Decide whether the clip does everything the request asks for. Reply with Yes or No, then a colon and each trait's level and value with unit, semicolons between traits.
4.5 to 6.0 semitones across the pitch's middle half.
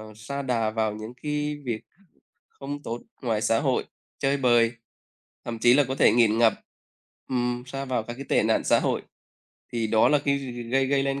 No: average, 3.2 semitones